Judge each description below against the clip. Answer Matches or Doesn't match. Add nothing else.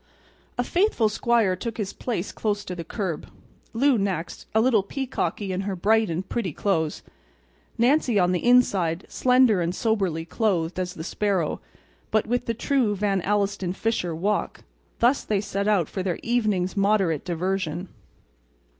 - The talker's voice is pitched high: Matches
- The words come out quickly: Doesn't match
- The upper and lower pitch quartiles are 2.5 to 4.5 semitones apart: Matches